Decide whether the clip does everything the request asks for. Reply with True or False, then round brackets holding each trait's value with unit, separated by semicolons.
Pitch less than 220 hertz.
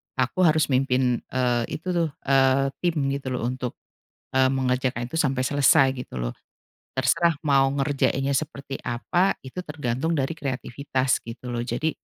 True (135 Hz)